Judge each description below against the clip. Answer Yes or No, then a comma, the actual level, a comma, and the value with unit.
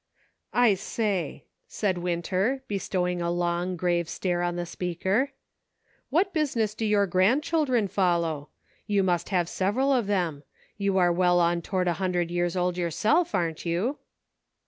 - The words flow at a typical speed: Yes, average, 150 wpm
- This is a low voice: No, medium, 185 Hz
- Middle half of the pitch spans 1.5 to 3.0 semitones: No, average, 3.4 semitones